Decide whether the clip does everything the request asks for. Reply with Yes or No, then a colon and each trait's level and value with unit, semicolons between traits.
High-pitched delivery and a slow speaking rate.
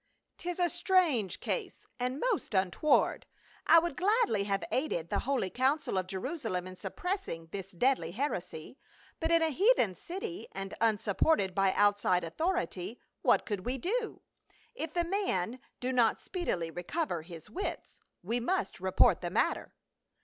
No: high, 240 Hz; average, 165 wpm